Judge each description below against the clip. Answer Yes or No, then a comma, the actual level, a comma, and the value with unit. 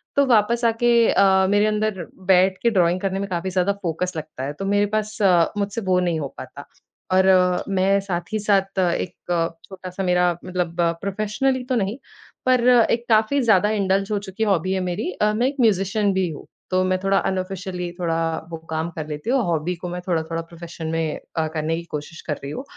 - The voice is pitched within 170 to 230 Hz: Yes, high, 190 Hz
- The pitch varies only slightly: No, average, 3.4 semitones